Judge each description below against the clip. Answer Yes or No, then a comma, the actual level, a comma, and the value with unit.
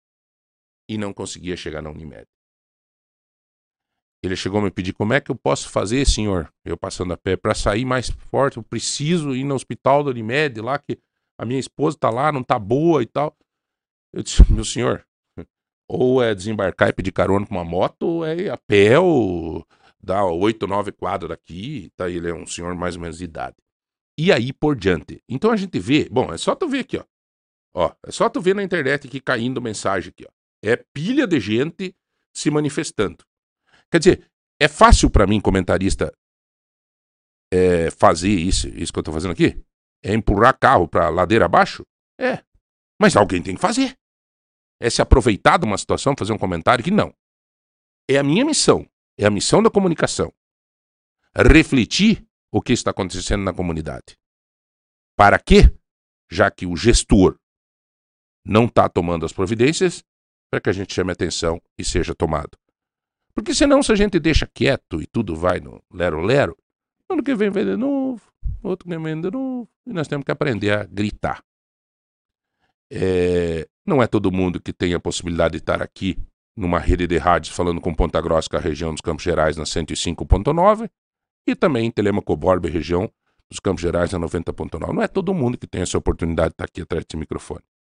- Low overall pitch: Yes, low, 105 Hz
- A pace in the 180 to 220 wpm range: Yes, fast, 185 wpm